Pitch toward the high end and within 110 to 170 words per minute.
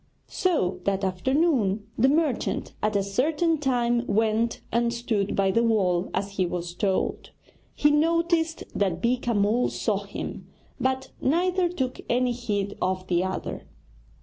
Yes: high, 235 Hz; average, 145 wpm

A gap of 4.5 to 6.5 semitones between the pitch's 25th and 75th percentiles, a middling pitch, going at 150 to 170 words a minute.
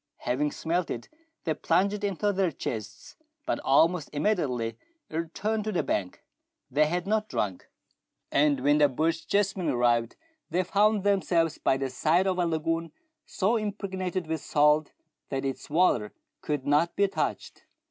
Yes: average, 4.9 semitones; medium, 165 Hz; average, 155 wpm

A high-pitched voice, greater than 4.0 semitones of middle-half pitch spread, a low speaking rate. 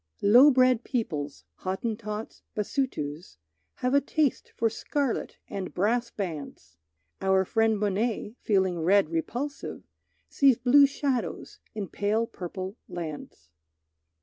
Yes: high, 210 Hz; average, 5.0 semitones; slow, 110 wpm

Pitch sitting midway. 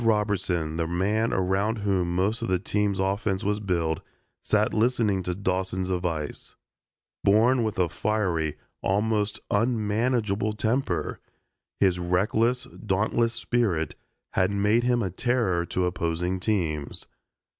No: low, 100 Hz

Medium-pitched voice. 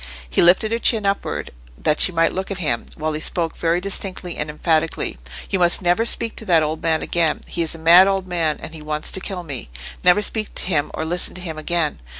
Yes: medium, 170 Hz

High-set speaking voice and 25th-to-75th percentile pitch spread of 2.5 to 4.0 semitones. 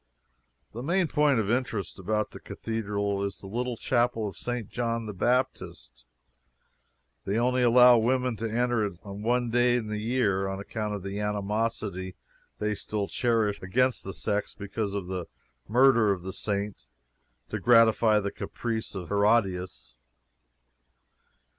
No: low, 110 Hz; average, 3.3 semitones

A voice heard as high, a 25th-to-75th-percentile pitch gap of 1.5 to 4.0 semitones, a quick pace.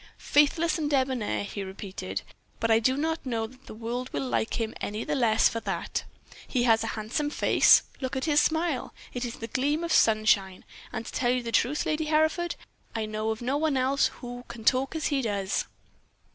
No: high, 245 Hz; average, 4.7 semitones; fast, 210 wpm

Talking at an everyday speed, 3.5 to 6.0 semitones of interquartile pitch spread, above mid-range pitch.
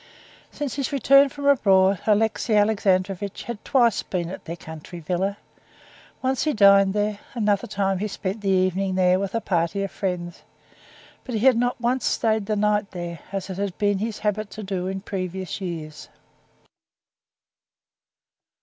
No: average, 160 wpm; average, 2.8 semitones; high, 200 Hz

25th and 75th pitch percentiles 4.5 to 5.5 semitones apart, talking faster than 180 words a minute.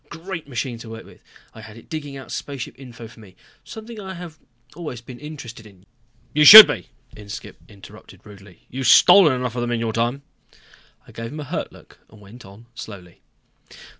Yes: average, 5.0 semitones; average, 195 wpm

